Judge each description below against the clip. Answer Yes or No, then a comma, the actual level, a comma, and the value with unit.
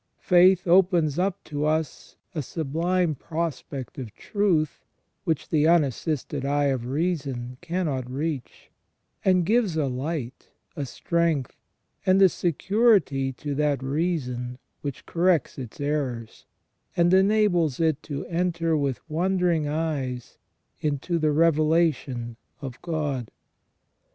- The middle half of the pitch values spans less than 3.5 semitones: No, average, 4.1 semitones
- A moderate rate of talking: No, slow, 115 wpm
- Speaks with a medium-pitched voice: Yes, medium, 155 Hz